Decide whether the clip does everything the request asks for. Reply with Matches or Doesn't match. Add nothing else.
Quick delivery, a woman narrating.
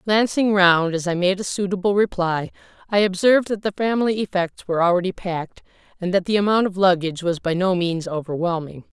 Doesn't match